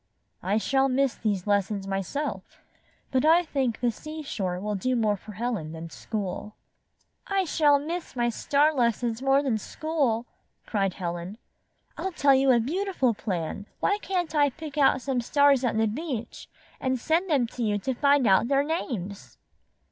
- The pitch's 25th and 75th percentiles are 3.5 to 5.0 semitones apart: No, wide, 5.5 semitones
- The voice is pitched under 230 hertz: No, very high, 250 Hz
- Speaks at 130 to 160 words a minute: No, average, 170 wpm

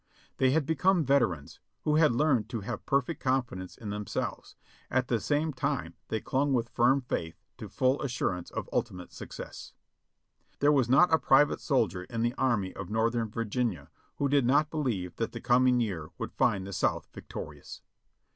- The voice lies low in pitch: Yes, low, 125 Hz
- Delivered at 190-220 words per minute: No, average, 175 wpm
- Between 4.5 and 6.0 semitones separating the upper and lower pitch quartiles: Yes, average, 5.0 semitones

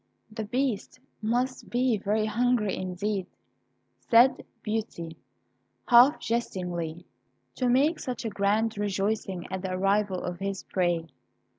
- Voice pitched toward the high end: Yes, high, 210 Hz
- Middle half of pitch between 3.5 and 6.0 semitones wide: Yes, average, 4.2 semitones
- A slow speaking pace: Yes, slow, 115 wpm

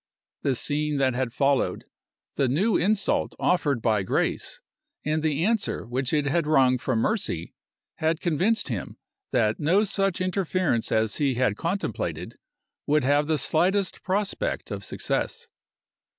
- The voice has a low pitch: No, medium, 150 Hz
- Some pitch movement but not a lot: No, wide, 6.2 semitones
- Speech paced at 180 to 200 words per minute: No, average, 140 wpm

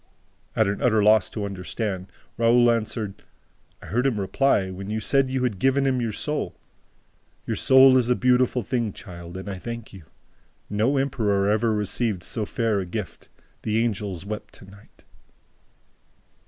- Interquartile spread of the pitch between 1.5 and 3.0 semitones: No, average, 3.7 semitones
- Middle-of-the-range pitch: No, low, 110 Hz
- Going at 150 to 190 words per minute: Yes, average, 160 wpm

